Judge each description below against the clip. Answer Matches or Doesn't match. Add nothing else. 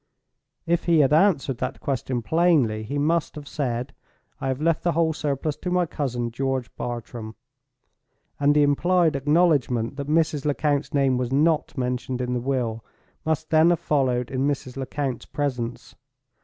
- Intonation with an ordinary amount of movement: Matches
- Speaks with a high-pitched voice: Doesn't match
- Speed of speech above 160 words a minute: Doesn't match